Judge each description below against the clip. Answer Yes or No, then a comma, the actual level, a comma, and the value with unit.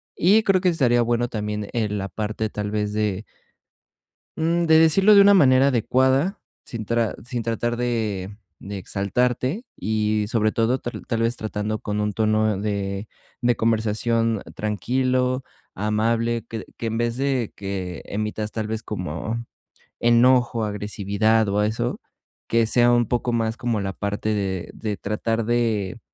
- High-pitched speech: No, low, 110 Hz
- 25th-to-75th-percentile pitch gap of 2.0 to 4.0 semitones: Yes, narrow, 2.5 semitones